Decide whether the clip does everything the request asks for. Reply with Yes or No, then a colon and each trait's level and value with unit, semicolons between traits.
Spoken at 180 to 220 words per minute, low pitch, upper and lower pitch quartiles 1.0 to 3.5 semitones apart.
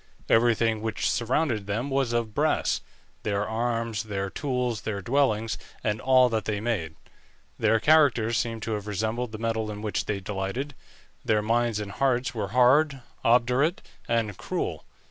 No: average, 155 wpm; low, 115 Hz; average, 2.7 semitones